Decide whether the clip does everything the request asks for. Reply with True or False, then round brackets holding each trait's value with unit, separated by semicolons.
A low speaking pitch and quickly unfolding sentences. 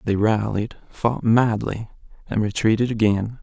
False (110 Hz; 125 wpm)